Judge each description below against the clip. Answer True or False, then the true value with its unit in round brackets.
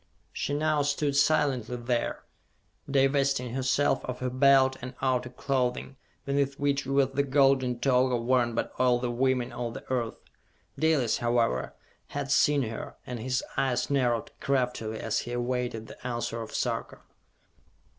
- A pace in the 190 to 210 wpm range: False (145 wpm)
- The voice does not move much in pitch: True (2.2 semitones)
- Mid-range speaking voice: False (130 Hz)